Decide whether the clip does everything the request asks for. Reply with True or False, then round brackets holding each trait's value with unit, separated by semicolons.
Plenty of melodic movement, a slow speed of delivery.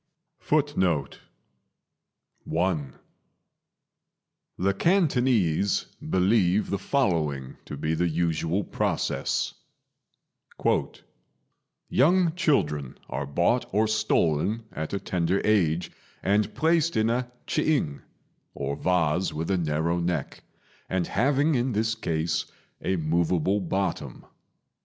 True (5.9 semitones; 95 wpm)